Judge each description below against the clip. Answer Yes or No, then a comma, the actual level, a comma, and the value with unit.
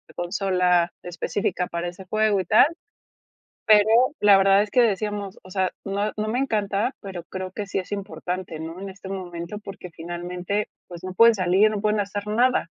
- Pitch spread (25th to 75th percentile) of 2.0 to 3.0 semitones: Yes, narrow, 2.6 semitones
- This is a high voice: Yes, high, 195 Hz